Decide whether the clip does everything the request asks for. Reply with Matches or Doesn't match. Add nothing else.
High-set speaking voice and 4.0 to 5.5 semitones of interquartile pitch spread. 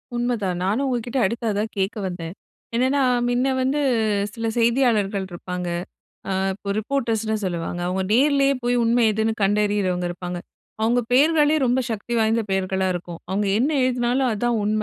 Matches